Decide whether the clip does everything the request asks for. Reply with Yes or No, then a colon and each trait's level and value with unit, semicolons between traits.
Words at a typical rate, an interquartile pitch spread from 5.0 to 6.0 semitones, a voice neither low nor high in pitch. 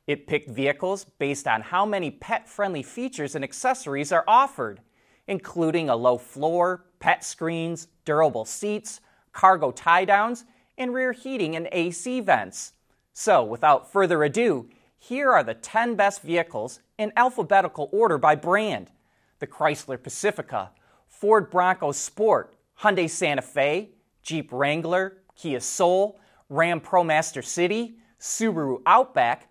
No: slow, 130 wpm; average, 5.3 semitones; medium, 180 Hz